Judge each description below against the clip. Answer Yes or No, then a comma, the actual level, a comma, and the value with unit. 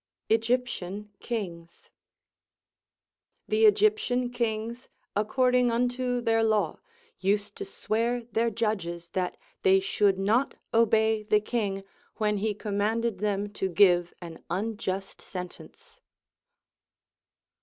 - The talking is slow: Yes, slow, 100 wpm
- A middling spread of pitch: Yes, average, 3.3 semitones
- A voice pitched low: No, high, 215 Hz